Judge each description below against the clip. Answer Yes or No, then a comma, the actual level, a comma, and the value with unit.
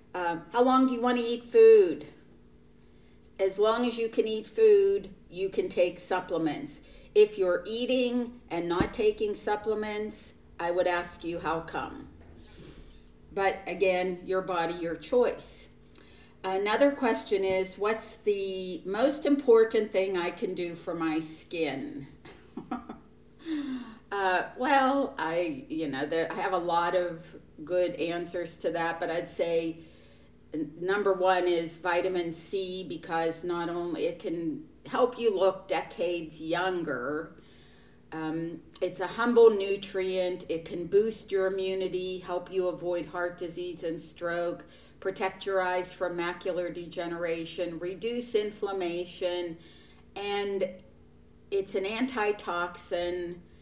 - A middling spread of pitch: Yes, average, 4.2 semitones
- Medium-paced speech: No, slow, 130 wpm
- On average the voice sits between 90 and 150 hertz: No, medium, 185 Hz